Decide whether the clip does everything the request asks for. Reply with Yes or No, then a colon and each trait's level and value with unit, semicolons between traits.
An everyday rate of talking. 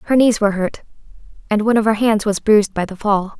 No: fast, 245 wpm